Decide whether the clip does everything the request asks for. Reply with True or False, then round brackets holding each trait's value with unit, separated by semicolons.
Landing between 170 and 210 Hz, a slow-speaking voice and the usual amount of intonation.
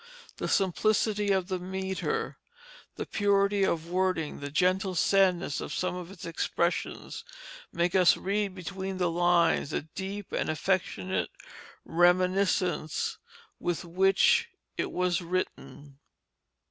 False (185 Hz; 115 wpm; 1.9 semitones)